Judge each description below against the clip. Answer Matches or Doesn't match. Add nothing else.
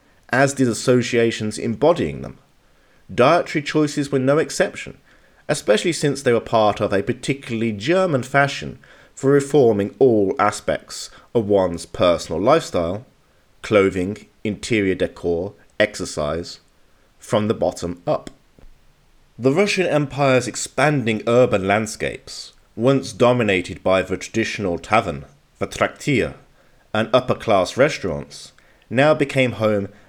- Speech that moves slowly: Matches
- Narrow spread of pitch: Doesn't match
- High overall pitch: Doesn't match